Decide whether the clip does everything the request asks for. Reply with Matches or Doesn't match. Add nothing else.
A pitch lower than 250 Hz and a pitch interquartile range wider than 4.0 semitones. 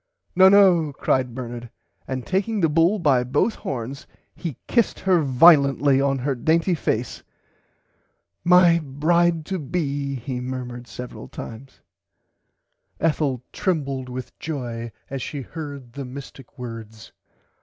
Matches